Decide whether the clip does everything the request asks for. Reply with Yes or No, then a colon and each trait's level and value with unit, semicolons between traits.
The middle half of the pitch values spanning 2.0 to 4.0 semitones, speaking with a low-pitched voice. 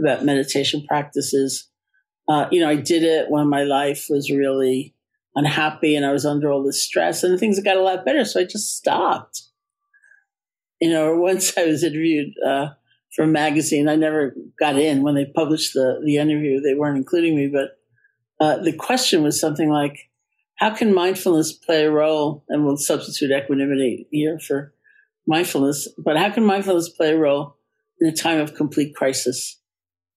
No: average, 3.4 semitones; medium, 150 Hz